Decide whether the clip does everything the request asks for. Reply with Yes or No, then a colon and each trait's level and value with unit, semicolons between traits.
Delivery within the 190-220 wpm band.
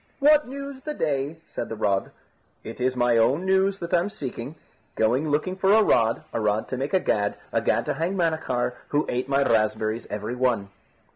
Yes: average, 200 wpm